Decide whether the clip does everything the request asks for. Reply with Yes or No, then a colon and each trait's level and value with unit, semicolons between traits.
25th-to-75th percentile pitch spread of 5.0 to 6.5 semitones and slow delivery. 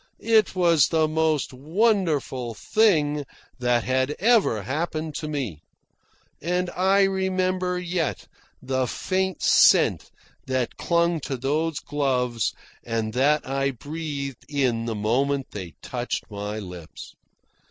Yes: wide, 5.6 semitones; slow, 120 wpm